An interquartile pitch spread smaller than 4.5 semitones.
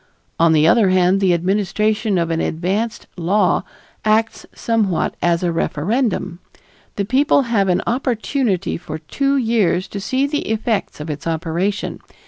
No: average, 4.8 semitones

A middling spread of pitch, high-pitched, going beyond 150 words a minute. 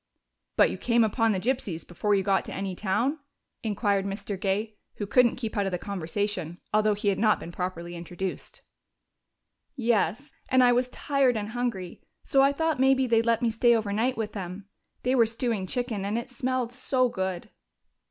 Yes: average, 4.1 semitones; high, 215 Hz; average, 185 wpm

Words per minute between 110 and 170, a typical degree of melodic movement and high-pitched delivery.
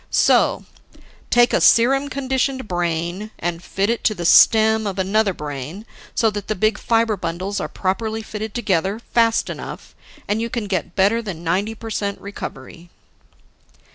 Yes: average, 160 wpm; average, 3.7 semitones; high, 205 Hz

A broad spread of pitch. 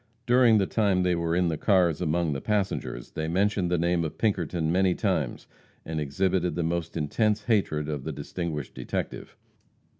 No: average, 3.6 semitones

